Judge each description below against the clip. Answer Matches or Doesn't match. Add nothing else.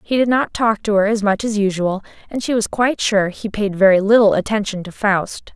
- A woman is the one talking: Matches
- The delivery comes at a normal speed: Doesn't match